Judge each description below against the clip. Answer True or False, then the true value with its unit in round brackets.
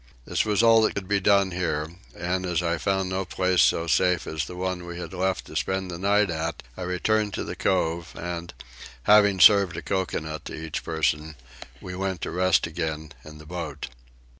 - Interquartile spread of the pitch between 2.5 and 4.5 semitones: True (2.8 semitones)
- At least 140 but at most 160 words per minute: False (200 wpm)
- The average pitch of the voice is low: True (90 Hz)